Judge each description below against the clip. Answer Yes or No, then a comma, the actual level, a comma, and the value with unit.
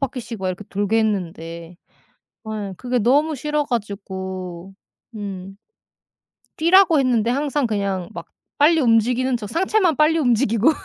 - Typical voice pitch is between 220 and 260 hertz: Yes, high, 225 Hz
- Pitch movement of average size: No, wide, 6.4 semitones